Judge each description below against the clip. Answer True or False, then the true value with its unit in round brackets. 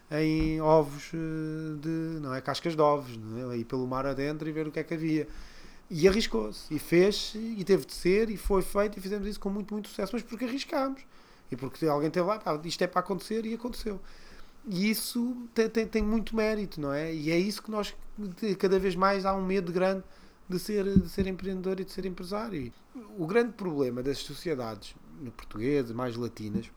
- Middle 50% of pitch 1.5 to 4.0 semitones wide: False (5.5 semitones)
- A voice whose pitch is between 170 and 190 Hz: True (185 Hz)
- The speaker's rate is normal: False (205 wpm)